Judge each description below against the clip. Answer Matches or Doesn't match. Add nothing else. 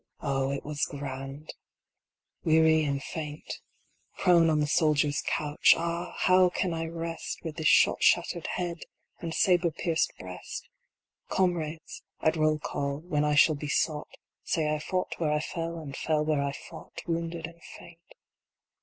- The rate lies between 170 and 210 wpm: Doesn't match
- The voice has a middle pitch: Matches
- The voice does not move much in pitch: Matches